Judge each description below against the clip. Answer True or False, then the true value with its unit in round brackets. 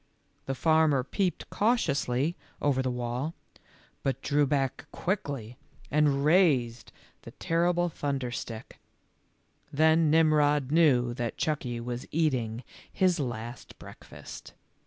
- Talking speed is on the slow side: True (120 wpm)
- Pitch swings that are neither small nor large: True (4.4 semitones)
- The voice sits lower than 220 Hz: True (140 Hz)